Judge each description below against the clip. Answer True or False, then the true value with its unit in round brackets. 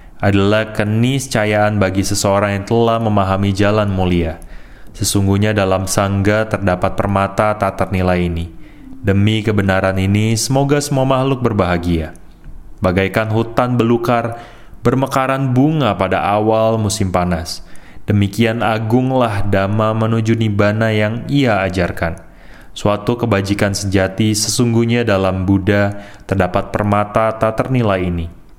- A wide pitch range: False (2.8 semitones)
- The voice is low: True (105 Hz)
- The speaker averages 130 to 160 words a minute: False (110 wpm)